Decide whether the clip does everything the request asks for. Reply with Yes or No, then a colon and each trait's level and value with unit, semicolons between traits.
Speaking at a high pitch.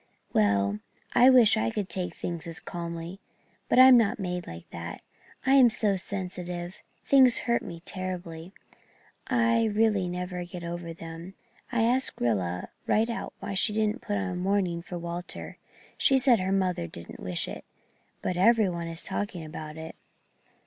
No: medium, 180 Hz